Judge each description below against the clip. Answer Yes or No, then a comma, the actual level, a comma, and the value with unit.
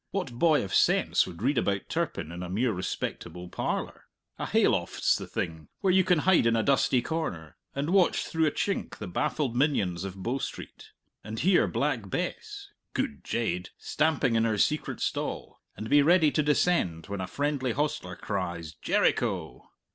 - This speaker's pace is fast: No, average, 175 wpm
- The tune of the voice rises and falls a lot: Yes, wide, 9.0 semitones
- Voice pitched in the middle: No, low, 125 Hz